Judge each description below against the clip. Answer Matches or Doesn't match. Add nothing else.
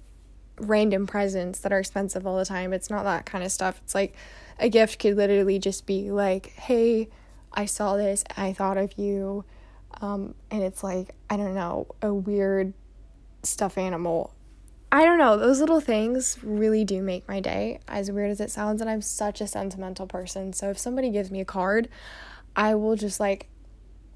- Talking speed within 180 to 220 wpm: Matches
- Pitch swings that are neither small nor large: Doesn't match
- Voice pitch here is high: Matches